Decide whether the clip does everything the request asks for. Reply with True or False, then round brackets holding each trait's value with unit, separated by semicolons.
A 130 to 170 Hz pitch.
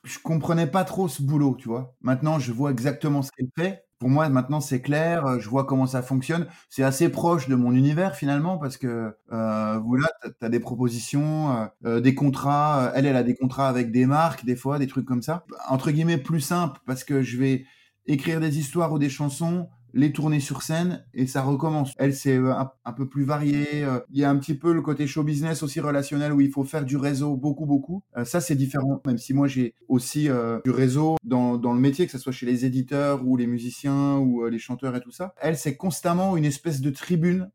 True (140 Hz)